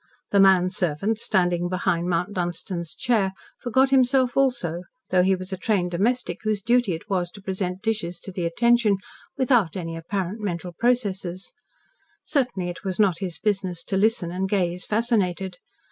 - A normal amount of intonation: Yes, average, 3.7 semitones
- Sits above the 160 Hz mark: Yes, high, 190 Hz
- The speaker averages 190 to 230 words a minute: No, average, 160 wpm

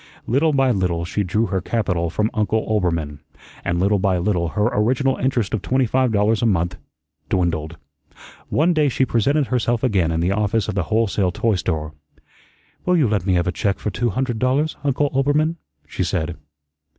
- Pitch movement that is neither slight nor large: No, wide, 6.1 semitones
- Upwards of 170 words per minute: Yes, average, 190 wpm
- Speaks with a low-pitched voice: Yes, low, 105 Hz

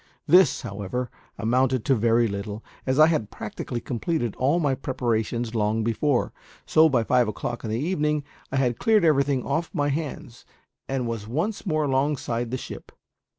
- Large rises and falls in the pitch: No, average, 4.5 semitones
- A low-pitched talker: Yes, low, 130 Hz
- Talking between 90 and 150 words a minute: No, average, 170 wpm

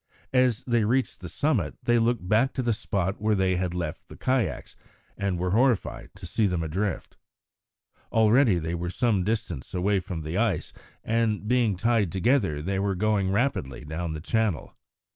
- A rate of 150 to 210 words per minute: Yes, average, 175 wpm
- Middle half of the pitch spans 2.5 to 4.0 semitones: No, average, 4.5 semitones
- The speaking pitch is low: Yes, low, 100 Hz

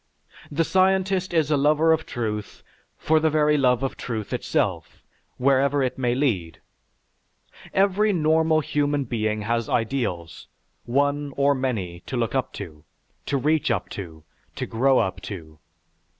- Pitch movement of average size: No, wide, 5.8 semitones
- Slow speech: No, average, 145 wpm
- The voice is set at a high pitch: No, low, 135 Hz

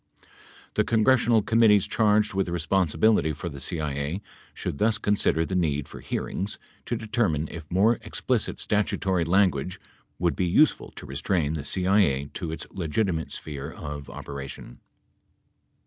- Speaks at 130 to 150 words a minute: Yes, average, 140 wpm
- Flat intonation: No, average, 5.3 semitones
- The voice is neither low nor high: No, very low, 90 Hz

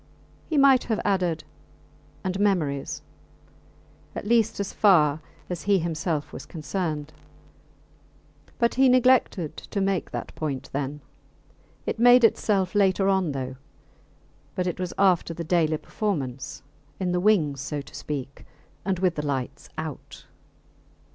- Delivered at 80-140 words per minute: Yes, slow, 135 wpm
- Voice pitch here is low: No, medium, 180 Hz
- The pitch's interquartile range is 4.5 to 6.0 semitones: Yes, average, 5.1 semitones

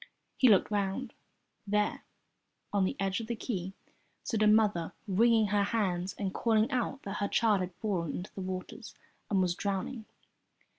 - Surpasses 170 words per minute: No, average, 165 wpm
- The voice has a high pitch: Yes, high, 200 Hz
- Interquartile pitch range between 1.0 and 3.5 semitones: Yes, average, 2.7 semitones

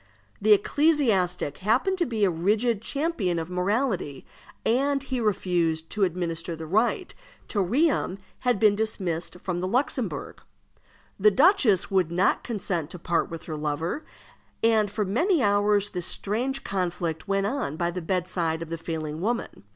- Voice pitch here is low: No, high, 195 Hz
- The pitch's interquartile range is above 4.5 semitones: Yes, average, 5.2 semitones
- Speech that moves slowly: No, average, 155 wpm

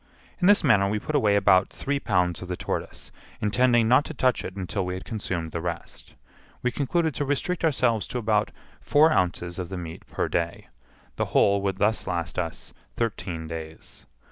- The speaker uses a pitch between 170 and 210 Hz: No, low, 100 Hz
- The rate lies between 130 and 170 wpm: No, average, 190 wpm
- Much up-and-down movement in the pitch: Yes, wide, 6.0 semitones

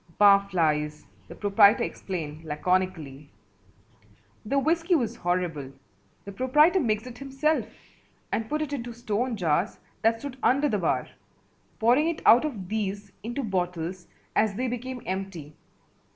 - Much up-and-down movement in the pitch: Yes, wide, 6.1 semitones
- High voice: Yes, high, 210 Hz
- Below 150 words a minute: Yes, slow, 135 wpm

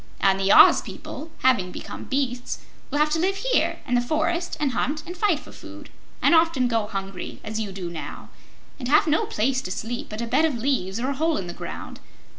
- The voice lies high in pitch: Yes, very high, 255 Hz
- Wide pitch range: Yes, wide, 6.5 semitones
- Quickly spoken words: Yes, fast, 225 wpm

